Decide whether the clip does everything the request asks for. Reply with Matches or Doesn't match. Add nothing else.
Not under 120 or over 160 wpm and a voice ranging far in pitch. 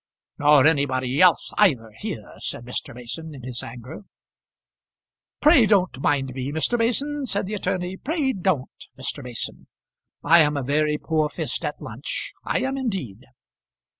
Matches